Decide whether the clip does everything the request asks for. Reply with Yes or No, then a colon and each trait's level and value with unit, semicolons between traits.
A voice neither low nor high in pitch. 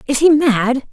No: very high, 265 Hz